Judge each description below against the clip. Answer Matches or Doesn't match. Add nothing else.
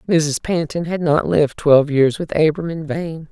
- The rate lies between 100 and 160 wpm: Doesn't match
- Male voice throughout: Doesn't match